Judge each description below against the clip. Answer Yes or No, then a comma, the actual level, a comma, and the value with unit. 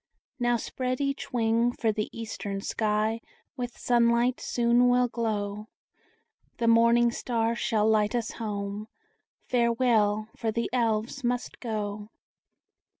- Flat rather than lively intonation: Yes, narrow, 2.1 semitones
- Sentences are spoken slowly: Yes, slow, 120 wpm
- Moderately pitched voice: No, high, 230 Hz